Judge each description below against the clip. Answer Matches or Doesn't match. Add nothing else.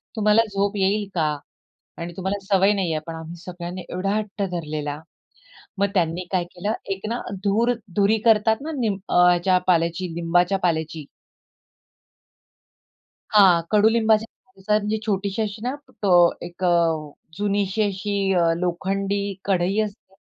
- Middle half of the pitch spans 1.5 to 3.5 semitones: Matches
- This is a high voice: Matches